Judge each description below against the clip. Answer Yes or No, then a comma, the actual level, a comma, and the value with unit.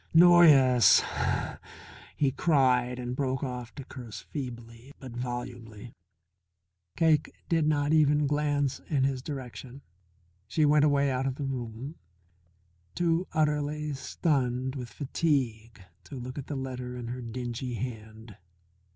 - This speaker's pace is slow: Yes, slow, 130 wpm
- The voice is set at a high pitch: No, low, 130 Hz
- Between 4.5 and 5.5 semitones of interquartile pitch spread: No, average, 3.1 semitones